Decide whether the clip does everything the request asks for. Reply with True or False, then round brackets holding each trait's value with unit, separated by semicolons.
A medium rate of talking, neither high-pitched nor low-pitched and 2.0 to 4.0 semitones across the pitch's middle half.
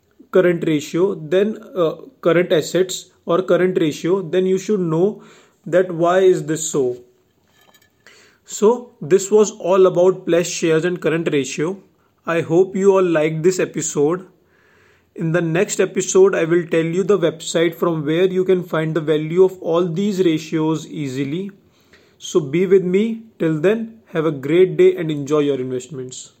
True (160 wpm; 175 Hz; 3.0 semitones)